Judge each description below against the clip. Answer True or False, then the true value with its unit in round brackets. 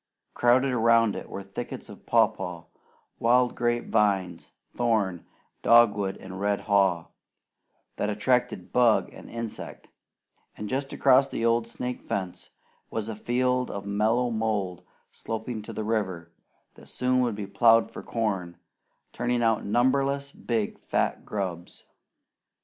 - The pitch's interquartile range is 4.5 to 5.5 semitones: False (3.3 semitones)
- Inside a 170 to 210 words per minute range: False (135 wpm)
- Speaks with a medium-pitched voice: False (110 Hz)